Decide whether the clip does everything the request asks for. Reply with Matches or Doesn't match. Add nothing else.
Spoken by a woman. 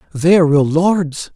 Doesn't match